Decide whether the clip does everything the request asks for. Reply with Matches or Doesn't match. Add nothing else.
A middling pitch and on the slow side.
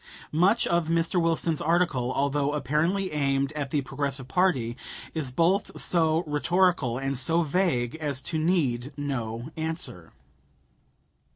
Matches